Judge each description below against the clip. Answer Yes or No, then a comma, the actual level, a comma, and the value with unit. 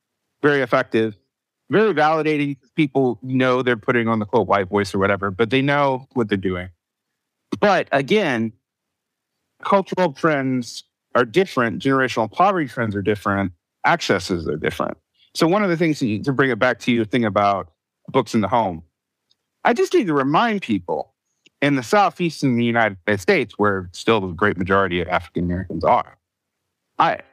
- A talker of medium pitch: No, low, 120 Hz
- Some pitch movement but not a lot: No, wide, 5.7 semitones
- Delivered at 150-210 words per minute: Yes, average, 170 wpm